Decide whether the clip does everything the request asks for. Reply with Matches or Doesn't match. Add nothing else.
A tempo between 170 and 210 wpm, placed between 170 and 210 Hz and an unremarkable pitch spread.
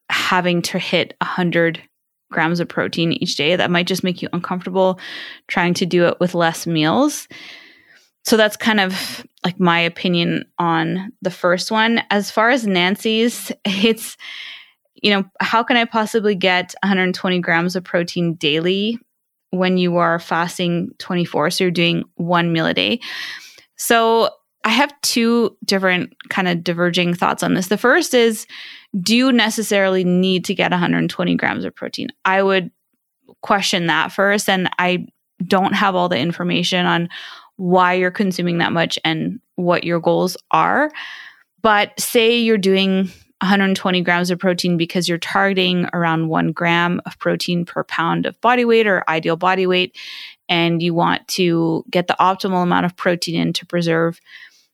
Doesn't match